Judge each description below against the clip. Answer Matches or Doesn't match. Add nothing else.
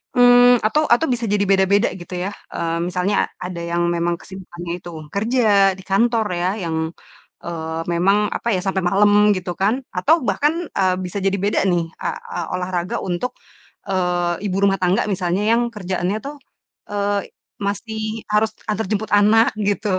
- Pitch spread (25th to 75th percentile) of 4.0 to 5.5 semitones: Doesn't match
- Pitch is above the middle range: Matches